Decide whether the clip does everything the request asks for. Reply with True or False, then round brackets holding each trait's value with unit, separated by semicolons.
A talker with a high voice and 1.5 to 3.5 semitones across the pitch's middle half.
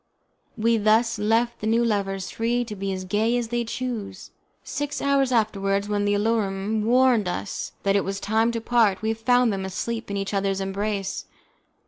True (215 Hz; 2.9 semitones)